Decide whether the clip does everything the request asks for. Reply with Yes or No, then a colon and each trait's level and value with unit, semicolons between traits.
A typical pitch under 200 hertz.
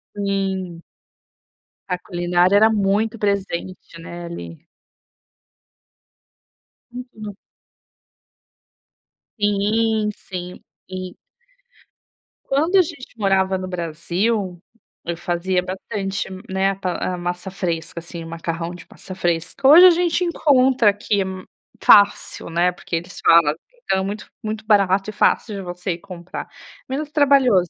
Yes: high, 190 Hz